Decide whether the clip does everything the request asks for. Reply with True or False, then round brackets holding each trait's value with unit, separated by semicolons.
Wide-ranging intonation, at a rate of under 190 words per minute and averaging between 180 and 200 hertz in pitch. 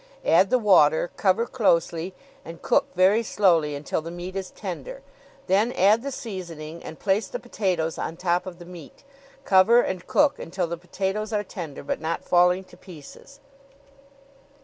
False (3.8 semitones; 165 wpm; 185 Hz)